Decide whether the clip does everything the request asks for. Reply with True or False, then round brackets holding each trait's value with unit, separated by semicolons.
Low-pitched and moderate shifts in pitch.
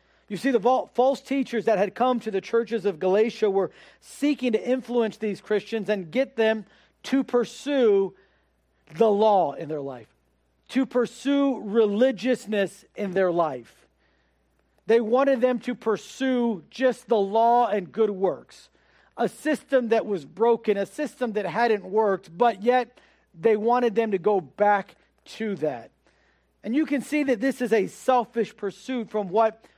False (225 Hz; 3.9 semitones)